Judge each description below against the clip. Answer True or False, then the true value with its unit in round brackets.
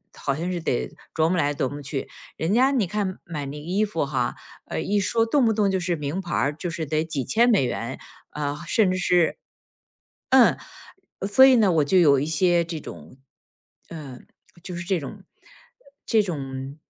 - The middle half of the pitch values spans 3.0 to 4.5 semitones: False (5.4 semitones)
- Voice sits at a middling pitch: True (170 Hz)